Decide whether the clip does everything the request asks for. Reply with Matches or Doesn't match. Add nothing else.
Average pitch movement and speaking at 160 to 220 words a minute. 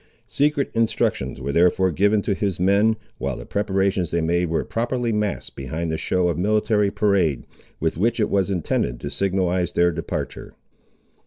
Matches